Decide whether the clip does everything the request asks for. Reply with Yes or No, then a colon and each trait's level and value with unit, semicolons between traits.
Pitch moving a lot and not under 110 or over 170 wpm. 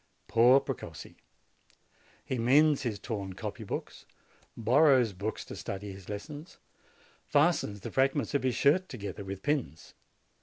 Yes: wide, 5.8 semitones; average, 140 wpm